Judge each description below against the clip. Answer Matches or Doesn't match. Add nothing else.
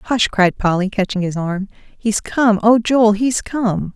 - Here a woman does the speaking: Matches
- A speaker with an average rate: Matches